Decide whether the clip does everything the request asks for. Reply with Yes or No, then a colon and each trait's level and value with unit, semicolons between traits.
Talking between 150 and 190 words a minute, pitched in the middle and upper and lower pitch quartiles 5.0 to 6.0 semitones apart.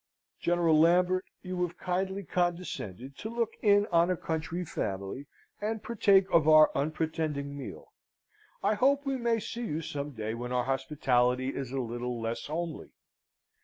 Yes: average, 155 wpm; medium, 160 Hz; wide, 5.6 semitones